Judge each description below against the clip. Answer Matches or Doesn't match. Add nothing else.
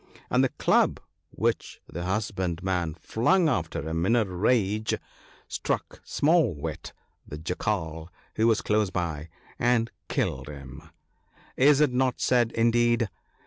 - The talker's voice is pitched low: Matches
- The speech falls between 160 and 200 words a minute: Doesn't match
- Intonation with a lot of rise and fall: Matches